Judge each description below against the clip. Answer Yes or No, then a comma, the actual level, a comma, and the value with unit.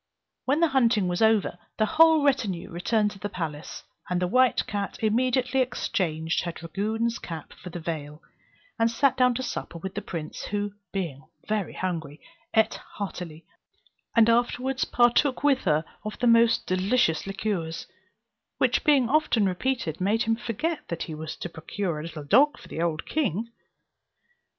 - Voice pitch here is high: Yes, high, 210 Hz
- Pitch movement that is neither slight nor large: No, wide, 6.3 semitones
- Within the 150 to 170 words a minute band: Yes, average, 165 wpm